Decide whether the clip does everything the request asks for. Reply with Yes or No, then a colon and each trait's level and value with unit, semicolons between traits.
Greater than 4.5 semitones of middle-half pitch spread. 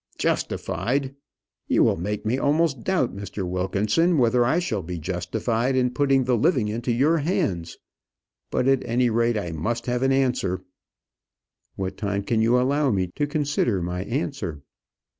Yes: average, 5.3 semitones